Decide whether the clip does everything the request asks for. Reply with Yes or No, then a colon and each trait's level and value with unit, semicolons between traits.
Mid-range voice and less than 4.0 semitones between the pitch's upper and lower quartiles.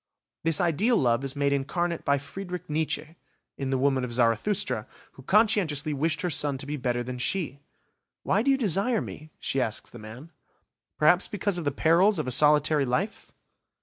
No: medium, 150 Hz; average, 5.1 semitones